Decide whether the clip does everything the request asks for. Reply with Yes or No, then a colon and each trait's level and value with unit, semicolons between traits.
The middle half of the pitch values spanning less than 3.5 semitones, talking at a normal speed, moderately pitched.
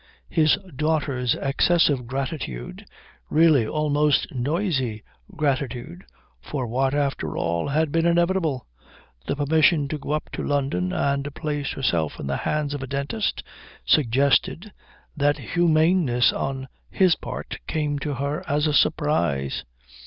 No: average, 2.8 semitones; slow, 130 wpm; medium, 145 Hz